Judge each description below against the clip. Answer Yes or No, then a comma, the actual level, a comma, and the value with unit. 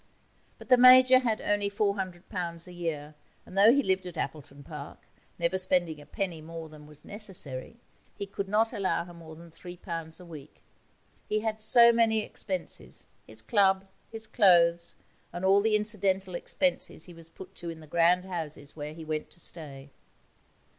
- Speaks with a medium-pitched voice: Yes, medium, 180 Hz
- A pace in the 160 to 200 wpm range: Yes, average, 175 wpm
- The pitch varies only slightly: No, average, 4.1 semitones